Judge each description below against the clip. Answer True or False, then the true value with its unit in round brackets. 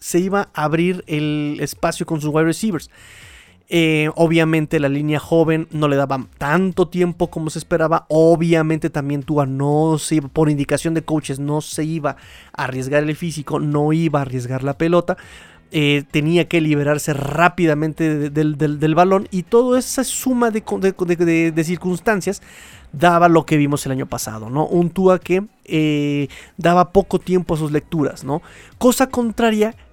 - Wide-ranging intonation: False (3.0 semitones)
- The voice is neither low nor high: True (160 Hz)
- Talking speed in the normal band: True (175 wpm)